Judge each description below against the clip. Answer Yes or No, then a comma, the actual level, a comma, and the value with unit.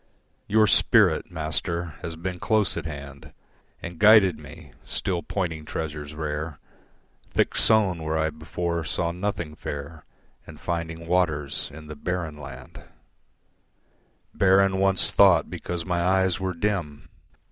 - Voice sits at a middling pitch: No, very low, 85 Hz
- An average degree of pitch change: Yes, average, 3.1 semitones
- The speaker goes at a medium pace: No, slow, 130 wpm